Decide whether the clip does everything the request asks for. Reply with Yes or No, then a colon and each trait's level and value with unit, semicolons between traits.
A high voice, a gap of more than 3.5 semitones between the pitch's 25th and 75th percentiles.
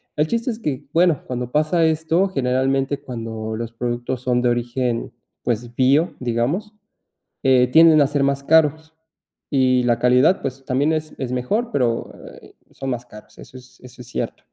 No: low, 130 Hz; average, 4.1 semitones